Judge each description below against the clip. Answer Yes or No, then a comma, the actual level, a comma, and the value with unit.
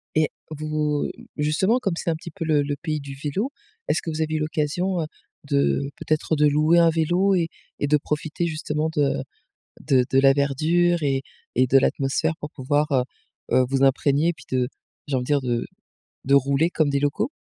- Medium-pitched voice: Yes, medium, 150 Hz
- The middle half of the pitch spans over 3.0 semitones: No, narrow, 2.6 semitones